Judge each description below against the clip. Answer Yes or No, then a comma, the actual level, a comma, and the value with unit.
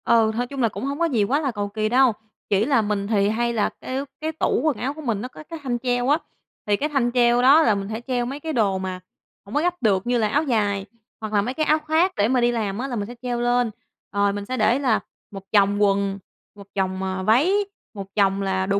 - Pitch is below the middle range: No, high, 230 Hz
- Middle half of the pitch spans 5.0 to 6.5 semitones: No, average, 4.5 semitones